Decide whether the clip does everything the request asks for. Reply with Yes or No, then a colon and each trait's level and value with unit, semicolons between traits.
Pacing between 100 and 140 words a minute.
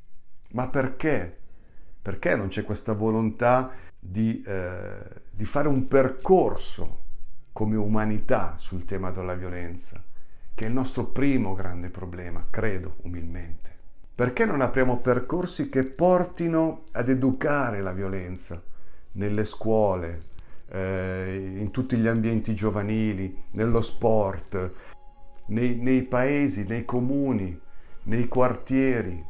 Yes: slow, 115 wpm